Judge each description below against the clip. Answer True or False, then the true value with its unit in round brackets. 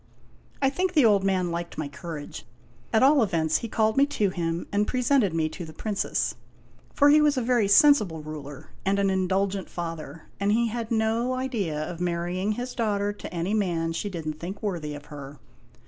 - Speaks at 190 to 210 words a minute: True (200 wpm)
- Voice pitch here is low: False (195 Hz)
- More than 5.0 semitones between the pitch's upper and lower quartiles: True (5.5 semitones)